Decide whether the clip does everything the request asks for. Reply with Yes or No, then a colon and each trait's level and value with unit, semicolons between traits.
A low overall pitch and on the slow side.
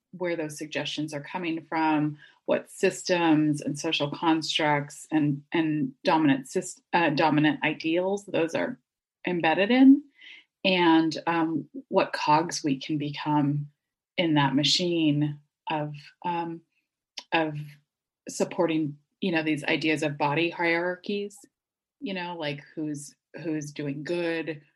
No: medium, 160 Hz; slow, 120 wpm